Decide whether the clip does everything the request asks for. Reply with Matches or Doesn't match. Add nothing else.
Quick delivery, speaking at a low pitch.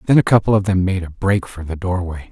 Matches